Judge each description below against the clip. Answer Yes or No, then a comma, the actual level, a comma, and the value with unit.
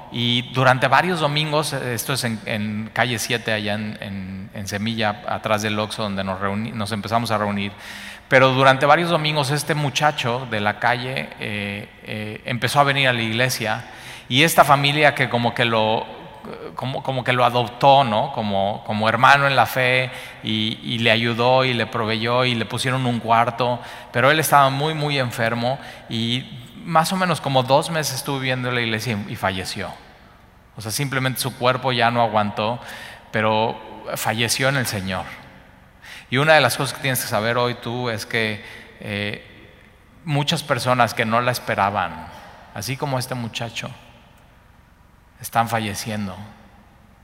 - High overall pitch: No, low, 120 Hz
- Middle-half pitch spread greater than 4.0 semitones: No, average, 3.5 semitones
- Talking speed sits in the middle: Yes, average, 170 wpm